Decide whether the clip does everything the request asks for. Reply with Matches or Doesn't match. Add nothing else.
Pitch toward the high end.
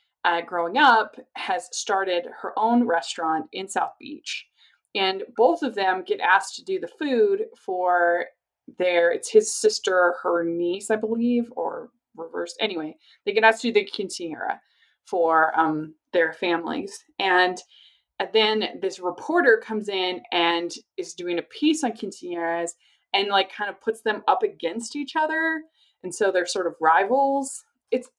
Matches